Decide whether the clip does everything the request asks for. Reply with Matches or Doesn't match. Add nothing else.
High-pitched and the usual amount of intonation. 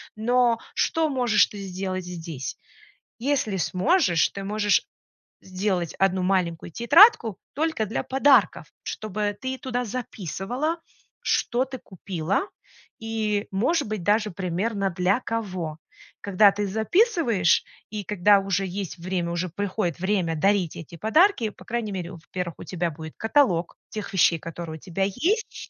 Matches